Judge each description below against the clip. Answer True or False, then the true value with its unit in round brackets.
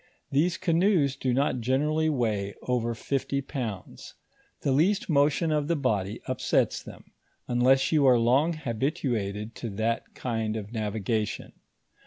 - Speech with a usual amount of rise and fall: True (4.8 semitones)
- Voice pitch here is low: True (130 Hz)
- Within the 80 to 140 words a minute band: True (135 wpm)